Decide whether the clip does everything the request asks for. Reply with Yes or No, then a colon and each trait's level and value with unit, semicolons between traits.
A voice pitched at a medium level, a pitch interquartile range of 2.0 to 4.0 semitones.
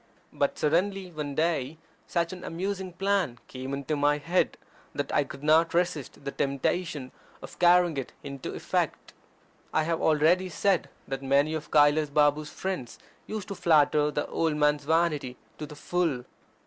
Yes: medium, 155 Hz; average, 3.4 semitones